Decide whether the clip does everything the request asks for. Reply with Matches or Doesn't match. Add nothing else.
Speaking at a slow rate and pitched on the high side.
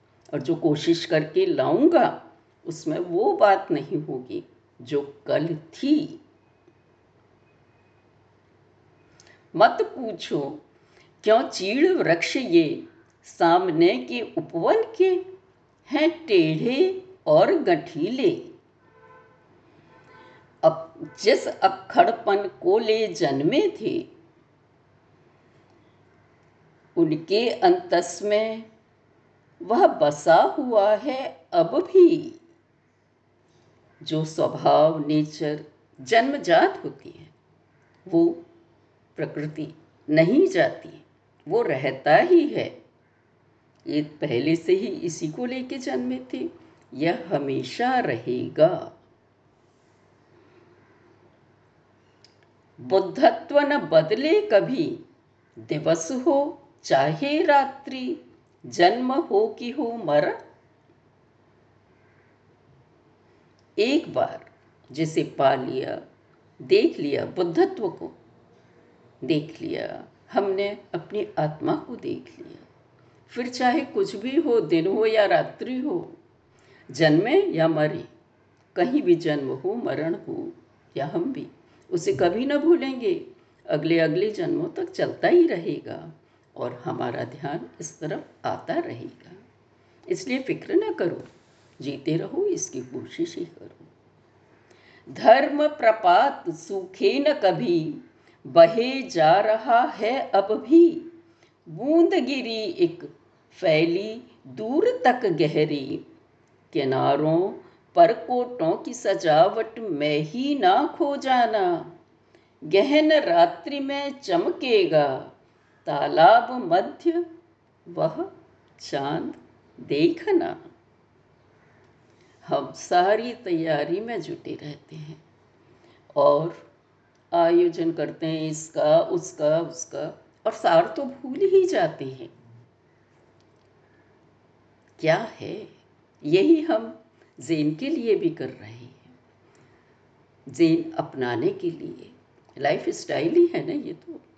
Matches